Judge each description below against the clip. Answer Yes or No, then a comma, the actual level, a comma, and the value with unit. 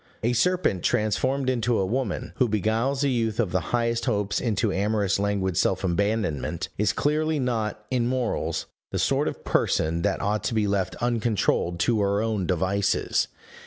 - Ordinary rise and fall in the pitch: Yes, average, 3.5 semitones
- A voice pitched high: No, low, 110 Hz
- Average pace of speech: Yes, average, 165 wpm